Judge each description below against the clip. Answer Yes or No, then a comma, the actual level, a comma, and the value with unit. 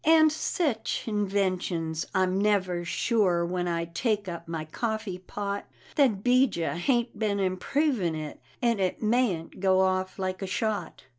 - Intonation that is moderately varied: Yes, average, 3.8 semitones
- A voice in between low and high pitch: No, high, 195 Hz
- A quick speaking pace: No, average, 145 wpm